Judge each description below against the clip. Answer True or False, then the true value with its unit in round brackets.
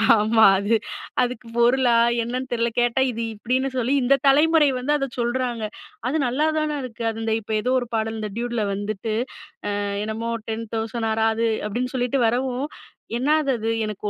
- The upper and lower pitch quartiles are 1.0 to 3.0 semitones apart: True (2.6 semitones)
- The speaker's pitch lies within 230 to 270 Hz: True (240 Hz)